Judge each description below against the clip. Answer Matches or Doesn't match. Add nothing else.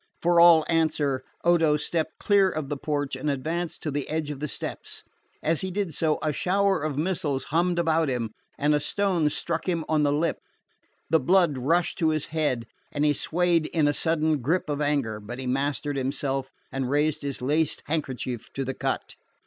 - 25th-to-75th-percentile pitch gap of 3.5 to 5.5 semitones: Doesn't match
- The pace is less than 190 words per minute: Doesn't match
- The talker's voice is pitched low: Doesn't match